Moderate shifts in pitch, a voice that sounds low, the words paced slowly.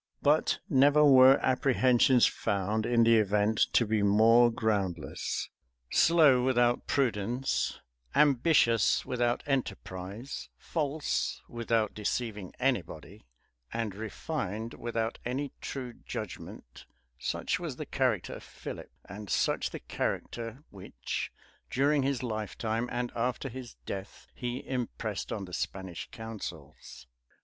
Yes: average, 3.7 semitones; low, 115 Hz; slow, 115 wpm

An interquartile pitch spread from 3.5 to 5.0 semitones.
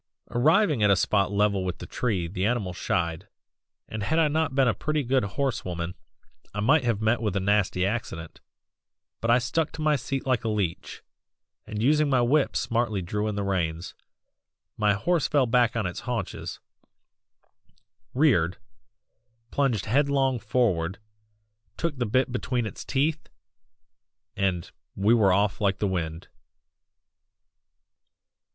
No: wide, 5.5 semitones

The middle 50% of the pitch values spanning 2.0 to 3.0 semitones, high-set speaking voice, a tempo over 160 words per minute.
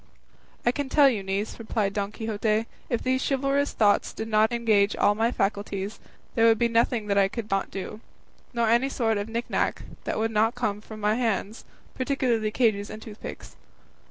Yes: narrow, 2.4 semitones; high, 220 Hz; average, 185 wpm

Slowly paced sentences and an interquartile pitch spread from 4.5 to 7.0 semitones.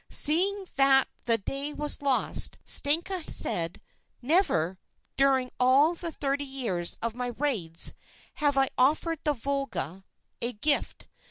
No: slow, 125 wpm; average, 3.8 semitones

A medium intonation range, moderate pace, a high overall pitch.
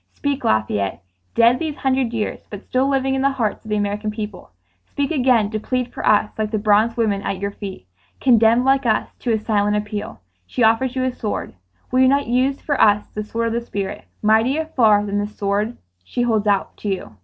No: average, 3.7 semitones; fast, 215 wpm; high, 220 Hz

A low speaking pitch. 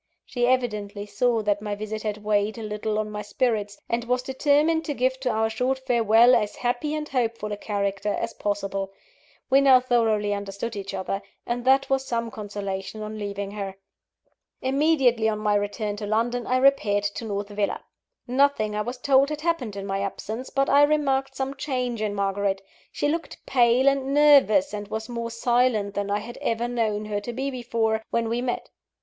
No: high, 225 Hz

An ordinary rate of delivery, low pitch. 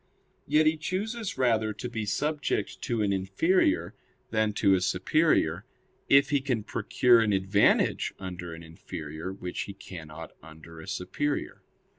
Yes: average, 145 wpm; low, 105 Hz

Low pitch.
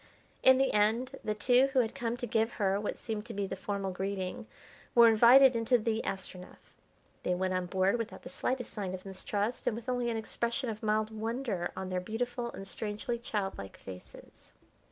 No: high, 220 Hz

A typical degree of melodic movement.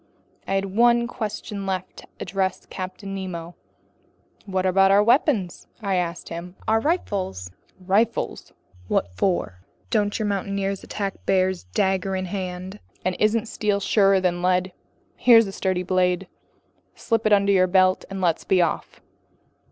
No: narrow, 2.0 semitones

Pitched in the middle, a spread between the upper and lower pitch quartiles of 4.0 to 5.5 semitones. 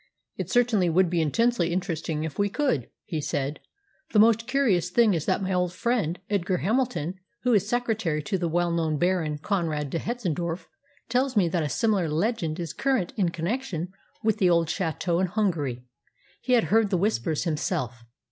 Yes: medium, 180 Hz; average, 5.1 semitones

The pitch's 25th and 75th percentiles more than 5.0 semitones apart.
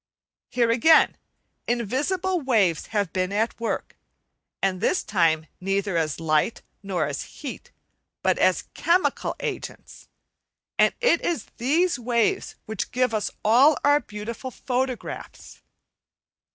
Yes: wide, 5.5 semitones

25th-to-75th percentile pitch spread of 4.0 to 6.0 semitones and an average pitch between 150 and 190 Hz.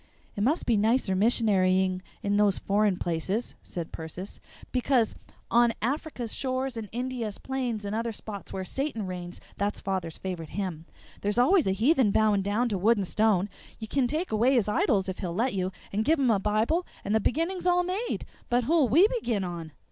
No: average, 4.9 semitones; high, 215 Hz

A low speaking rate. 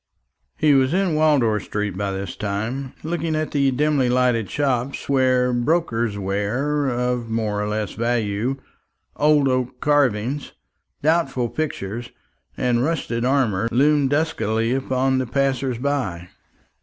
Yes: slow, 130 wpm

